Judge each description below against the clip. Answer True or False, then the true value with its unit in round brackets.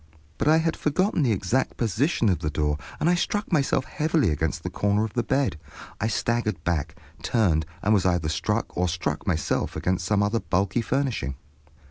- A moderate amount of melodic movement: False (7.4 semitones)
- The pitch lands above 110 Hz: False (105 Hz)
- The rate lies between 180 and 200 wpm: True (185 wpm)